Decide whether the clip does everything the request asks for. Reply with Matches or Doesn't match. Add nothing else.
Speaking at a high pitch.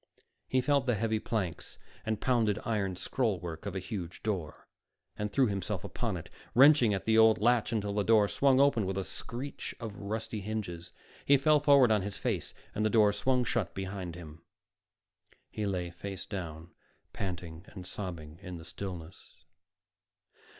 Doesn't match